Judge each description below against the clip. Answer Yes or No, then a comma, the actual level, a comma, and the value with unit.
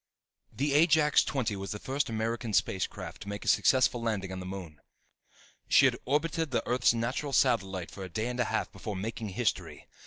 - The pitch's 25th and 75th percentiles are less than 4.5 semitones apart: No, average, 5.3 semitones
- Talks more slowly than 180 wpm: No, fast, 205 wpm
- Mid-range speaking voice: No, low, 115 Hz